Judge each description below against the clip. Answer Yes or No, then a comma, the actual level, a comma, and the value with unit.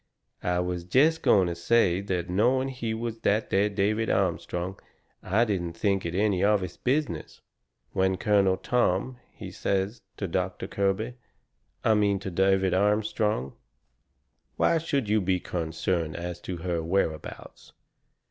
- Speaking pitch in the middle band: No, very low, 95 Hz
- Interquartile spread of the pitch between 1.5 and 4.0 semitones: Yes, average, 3.3 semitones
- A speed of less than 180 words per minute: Yes, average, 150 wpm